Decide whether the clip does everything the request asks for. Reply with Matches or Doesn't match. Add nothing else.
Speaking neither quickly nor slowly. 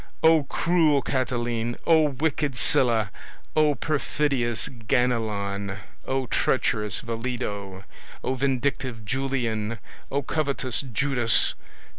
Doesn't match